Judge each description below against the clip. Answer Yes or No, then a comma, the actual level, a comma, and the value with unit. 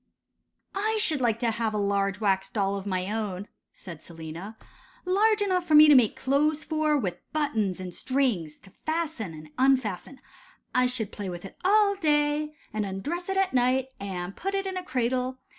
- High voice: Yes, very high, 250 Hz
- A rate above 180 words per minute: Yes, average, 190 wpm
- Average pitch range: No, wide, 7.7 semitones